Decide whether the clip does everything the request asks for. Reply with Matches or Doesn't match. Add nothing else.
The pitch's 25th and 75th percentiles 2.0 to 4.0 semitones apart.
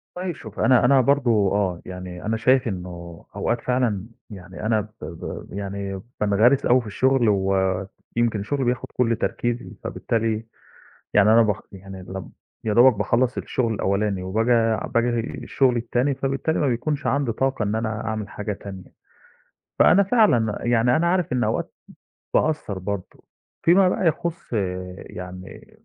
Doesn't match